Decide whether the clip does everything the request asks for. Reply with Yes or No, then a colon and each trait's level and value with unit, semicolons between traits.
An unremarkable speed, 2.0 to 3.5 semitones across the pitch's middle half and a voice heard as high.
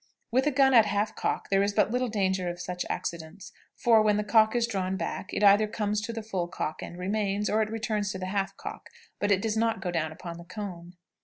No: fast, 240 wpm; average, 2.9 semitones; high, 205 Hz